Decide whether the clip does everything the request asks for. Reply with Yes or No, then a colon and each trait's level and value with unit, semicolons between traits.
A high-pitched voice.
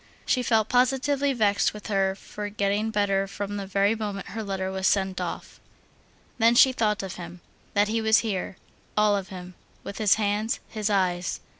Yes: high, 205 Hz